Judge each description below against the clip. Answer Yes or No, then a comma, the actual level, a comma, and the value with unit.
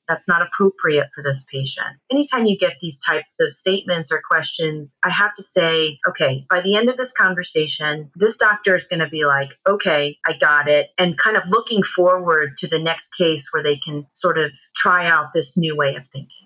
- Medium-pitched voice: Yes, medium, 165 Hz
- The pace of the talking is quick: Yes, fast, 210 wpm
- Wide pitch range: No, average, 3.9 semitones